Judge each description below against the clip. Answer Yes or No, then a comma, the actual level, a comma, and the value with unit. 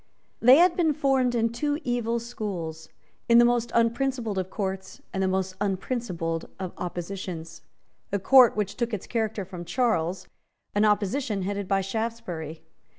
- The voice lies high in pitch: Yes, high, 210 Hz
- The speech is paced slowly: No, average, 150 wpm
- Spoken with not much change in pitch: No, average, 4.2 semitones